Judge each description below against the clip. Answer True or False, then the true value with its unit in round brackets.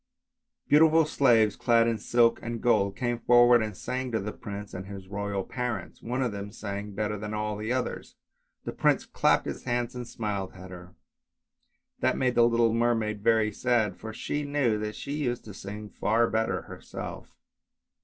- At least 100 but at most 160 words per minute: False (185 wpm)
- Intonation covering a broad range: False (2.8 semitones)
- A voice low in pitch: True (110 Hz)